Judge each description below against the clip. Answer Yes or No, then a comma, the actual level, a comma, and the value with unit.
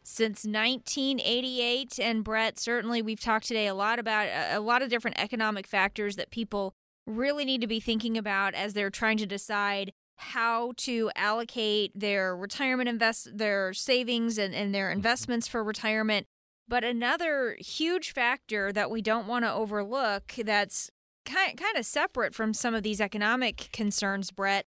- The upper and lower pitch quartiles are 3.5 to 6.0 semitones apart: No, average, 2.8 semitones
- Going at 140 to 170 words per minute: Yes, average, 160 wpm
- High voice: Yes, high, 225 Hz